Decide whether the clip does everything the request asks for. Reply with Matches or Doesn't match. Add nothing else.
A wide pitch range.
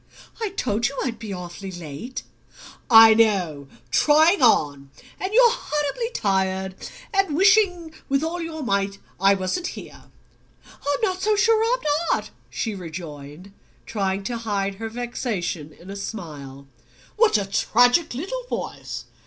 Matches